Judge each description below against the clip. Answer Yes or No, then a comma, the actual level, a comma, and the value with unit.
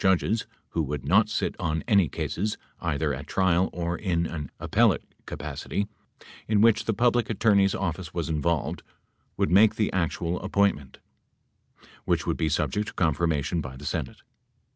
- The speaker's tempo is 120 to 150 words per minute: Yes, average, 140 wpm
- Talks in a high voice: No, very low, 85 Hz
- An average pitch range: Yes, average, 4.5 semitones